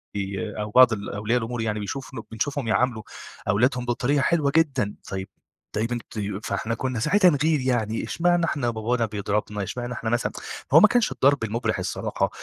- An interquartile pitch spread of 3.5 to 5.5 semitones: Yes, average, 4.3 semitones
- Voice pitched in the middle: No, low, 120 Hz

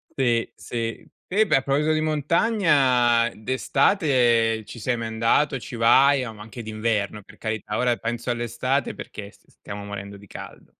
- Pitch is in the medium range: No, low, 120 Hz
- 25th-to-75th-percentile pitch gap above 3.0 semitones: Yes, average, 3.6 semitones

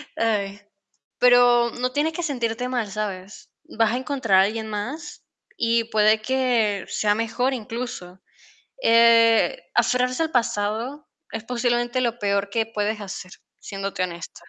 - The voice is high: Yes, high, 230 Hz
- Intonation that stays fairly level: No, average, 3.0 semitones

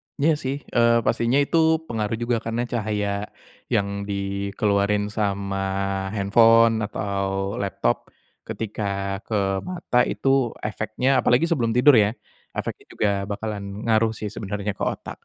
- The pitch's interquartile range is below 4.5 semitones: Yes, average, 2.8 semitones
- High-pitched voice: No, low, 105 Hz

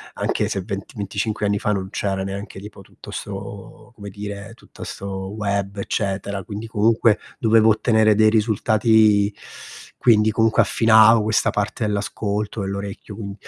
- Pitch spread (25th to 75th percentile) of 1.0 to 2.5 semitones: Yes, narrow, 1.7 semitones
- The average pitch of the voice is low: Yes, low, 105 Hz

